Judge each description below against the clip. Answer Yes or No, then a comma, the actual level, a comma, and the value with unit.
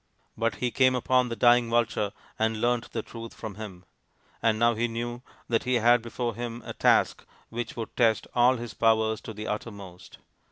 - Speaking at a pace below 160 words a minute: No, average, 190 wpm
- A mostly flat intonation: Yes, narrow, 1.6 semitones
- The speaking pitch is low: Yes, low, 115 Hz